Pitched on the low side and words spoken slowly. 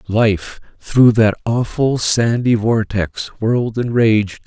Yes: low, 110 Hz; slow, 120 wpm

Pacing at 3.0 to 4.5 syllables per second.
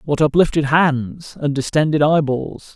Yes: 4.2 syllables/s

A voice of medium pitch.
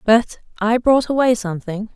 No: high, 225 Hz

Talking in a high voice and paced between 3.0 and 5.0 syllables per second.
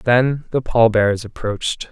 No: low, 115 Hz; 4.4 syllables/s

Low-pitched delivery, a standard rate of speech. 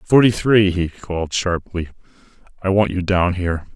Yes: very low, 95 Hz; average, 160 wpm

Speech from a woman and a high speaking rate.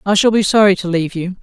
Yes: female; fast, 295 wpm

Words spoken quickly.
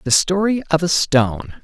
No: average, 185 wpm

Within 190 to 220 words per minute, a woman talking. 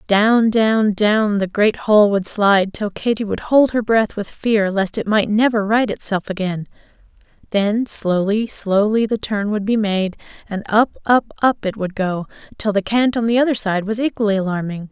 Yes: average, 195 wpm; female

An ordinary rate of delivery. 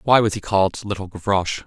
No: fast, 215 wpm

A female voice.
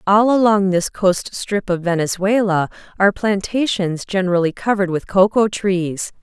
Yes: female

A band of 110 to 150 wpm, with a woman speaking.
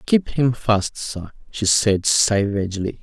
No: average, 140 wpm; male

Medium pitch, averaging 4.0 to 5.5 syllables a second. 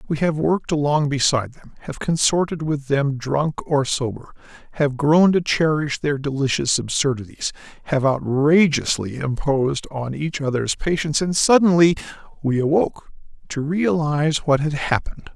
Yes: medium, 145 Hz; 4.9 syllables/s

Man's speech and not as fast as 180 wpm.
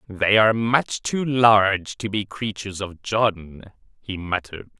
Yes: male; average, 150 wpm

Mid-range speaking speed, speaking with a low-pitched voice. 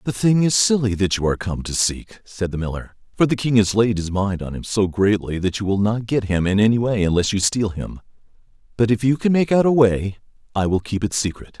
No: fast, 260 wpm; low, 105 Hz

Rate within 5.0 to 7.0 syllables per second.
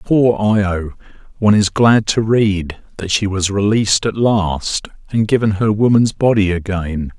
No: 4.3 syllables/s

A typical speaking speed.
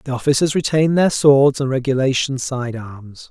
Yes: average, 165 wpm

